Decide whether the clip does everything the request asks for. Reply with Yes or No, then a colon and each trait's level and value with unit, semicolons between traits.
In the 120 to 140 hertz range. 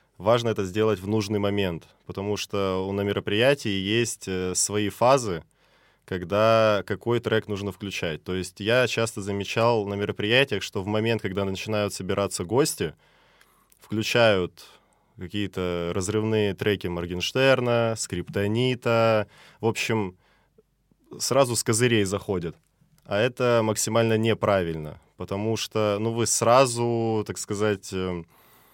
No: low, 105 Hz